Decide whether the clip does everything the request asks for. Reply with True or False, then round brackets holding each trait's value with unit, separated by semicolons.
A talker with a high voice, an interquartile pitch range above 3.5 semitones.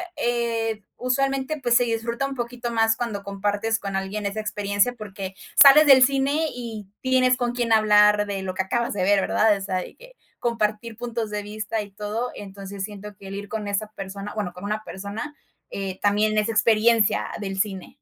False (215 Hz; 2.9 semitones)